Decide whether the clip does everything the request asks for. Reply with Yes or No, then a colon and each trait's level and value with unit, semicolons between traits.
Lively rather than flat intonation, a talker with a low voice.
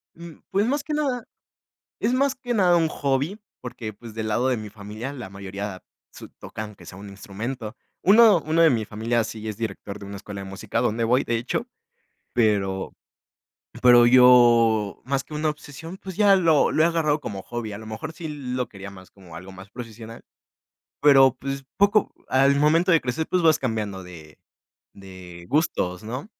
Yes: wide, 7.1 semitones; low, 120 Hz